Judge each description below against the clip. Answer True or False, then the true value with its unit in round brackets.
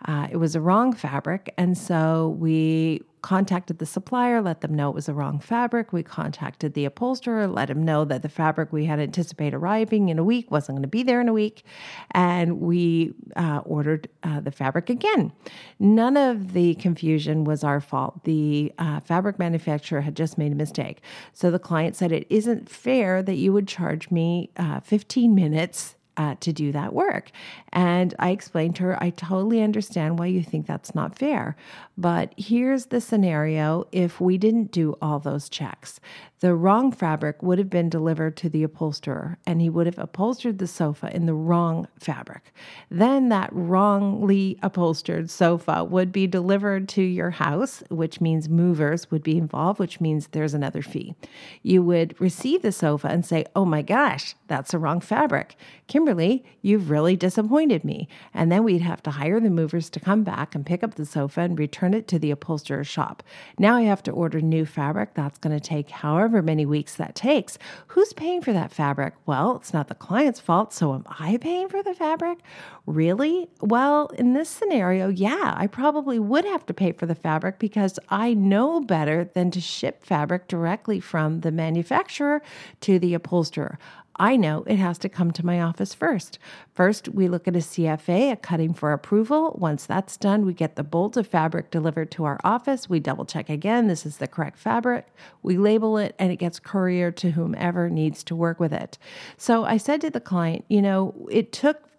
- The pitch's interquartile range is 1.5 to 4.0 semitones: False (4.8 semitones)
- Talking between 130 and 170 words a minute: False (195 wpm)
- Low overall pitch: False (175 Hz)